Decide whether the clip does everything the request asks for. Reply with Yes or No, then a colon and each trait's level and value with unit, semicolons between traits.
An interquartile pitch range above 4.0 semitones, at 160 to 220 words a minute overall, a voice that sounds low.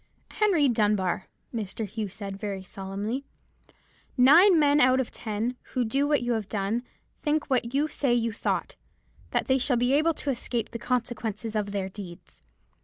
No: average, 4.6 semitones; average, 170 wpm; high, 235 Hz